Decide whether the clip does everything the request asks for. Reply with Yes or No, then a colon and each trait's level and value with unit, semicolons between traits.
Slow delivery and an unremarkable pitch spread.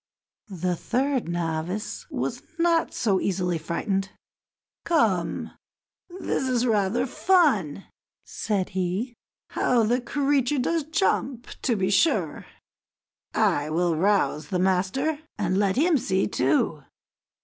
No: slow, 115 wpm; wide, 6.8 semitones